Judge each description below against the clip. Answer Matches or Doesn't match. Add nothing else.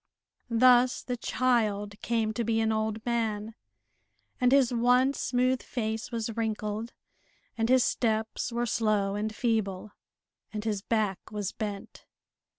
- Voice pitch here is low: Doesn't match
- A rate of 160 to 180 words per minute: Doesn't match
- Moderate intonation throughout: Doesn't match